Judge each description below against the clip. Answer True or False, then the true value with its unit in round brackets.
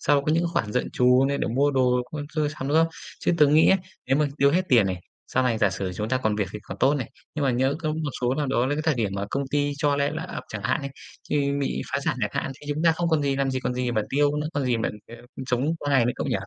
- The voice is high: False (140 Hz)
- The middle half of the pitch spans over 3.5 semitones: False (2.9 semitones)